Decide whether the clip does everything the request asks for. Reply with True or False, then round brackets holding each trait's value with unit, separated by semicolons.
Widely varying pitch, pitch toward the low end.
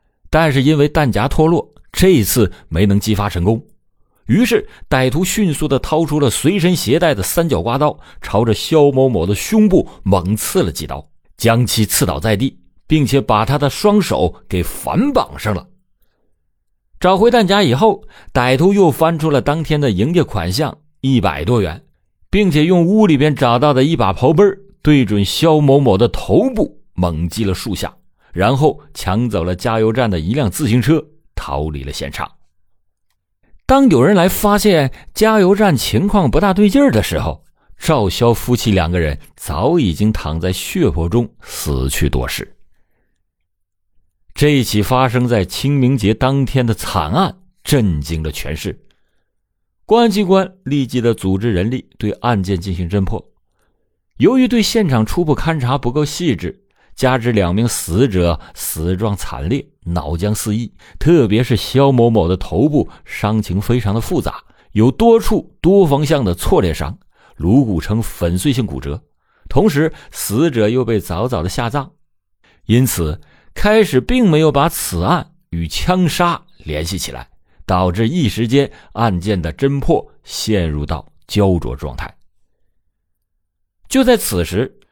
True (8.8 semitones; 115 Hz)